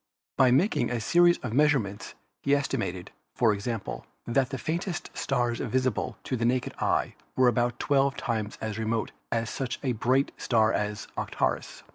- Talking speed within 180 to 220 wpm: No, average, 160 wpm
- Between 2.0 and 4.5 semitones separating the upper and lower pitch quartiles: Yes, average, 3.4 semitones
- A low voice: Yes, low, 125 Hz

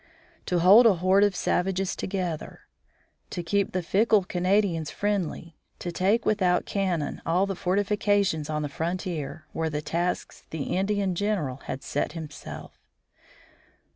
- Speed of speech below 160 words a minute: Yes, average, 140 wpm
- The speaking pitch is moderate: Yes, medium, 180 Hz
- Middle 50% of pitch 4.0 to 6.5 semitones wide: No, average, 3.6 semitones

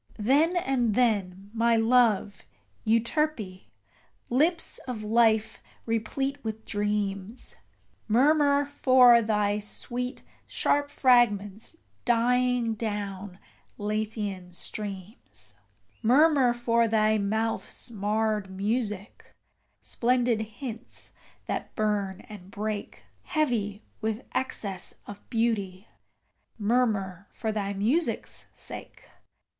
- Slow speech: Yes, slow, 90 wpm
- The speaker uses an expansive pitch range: No, average, 3.1 semitones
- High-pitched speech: Yes, high, 220 Hz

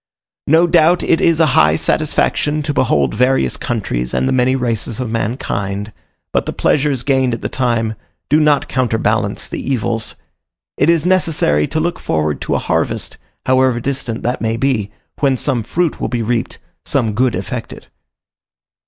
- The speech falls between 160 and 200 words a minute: Yes, average, 165 wpm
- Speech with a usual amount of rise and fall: Yes, average, 4.6 semitones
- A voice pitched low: Yes, low, 125 Hz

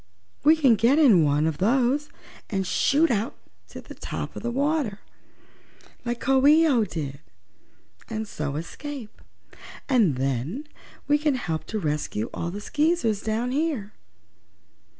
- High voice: Yes, high, 230 Hz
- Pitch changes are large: Yes, wide, 8.6 semitones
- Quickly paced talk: No, average, 145 wpm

